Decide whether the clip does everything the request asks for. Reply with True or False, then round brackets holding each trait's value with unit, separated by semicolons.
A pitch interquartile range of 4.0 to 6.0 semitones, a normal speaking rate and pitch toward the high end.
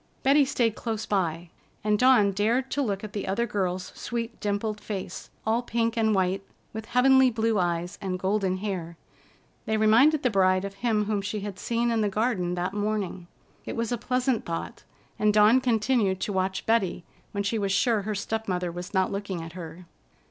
False (3.4 semitones; 190 wpm; 210 Hz)